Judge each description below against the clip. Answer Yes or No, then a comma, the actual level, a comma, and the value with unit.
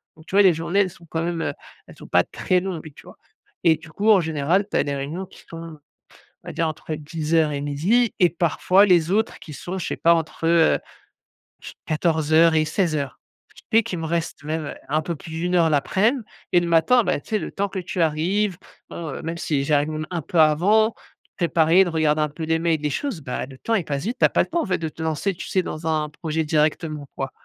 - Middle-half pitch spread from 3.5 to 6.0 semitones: No, average, 2.9 semitones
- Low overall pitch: No, medium, 165 Hz